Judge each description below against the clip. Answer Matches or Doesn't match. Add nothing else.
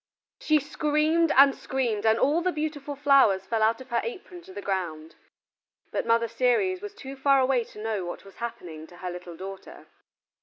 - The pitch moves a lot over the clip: Matches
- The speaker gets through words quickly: Doesn't match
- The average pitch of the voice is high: Matches